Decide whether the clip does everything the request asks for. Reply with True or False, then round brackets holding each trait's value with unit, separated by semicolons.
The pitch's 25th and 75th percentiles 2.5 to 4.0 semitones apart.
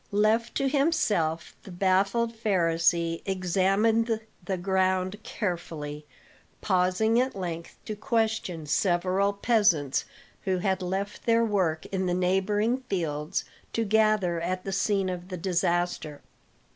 True (3.5 semitones)